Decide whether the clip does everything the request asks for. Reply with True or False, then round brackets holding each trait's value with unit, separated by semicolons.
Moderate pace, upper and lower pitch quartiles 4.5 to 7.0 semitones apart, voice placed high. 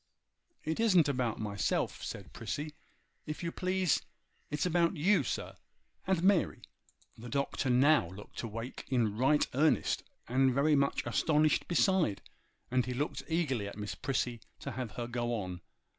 False (150 wpm; 5.2 semitones; 135 Hz)